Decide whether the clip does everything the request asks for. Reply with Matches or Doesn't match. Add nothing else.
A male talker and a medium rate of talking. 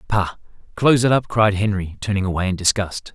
Matches